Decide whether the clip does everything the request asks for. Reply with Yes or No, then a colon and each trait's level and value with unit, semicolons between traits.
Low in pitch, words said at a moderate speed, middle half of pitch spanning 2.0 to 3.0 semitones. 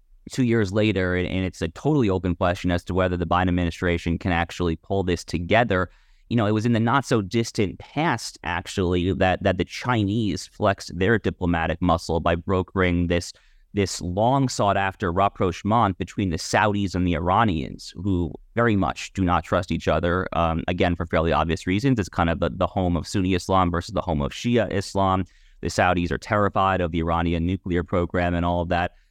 Yes: very low, 90 Hz; average, 195 wpm; narrow, 2.6 semitones